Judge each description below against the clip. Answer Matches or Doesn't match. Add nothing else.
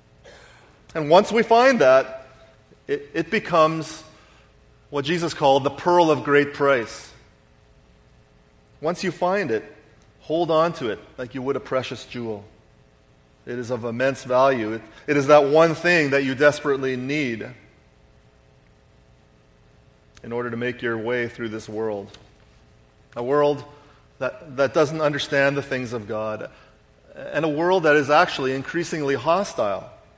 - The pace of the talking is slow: Doesn't match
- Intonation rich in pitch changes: Matches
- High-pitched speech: Doesn't match